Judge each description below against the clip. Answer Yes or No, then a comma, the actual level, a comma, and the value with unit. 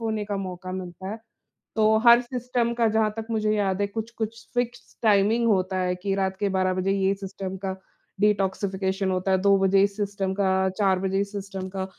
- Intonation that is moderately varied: No, narrow, 2.3 semitones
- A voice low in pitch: No, high, 195 Hz